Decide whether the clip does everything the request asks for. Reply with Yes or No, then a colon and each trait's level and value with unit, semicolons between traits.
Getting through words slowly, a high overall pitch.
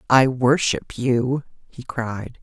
No: slow, 125 wpm; low, 125 Hz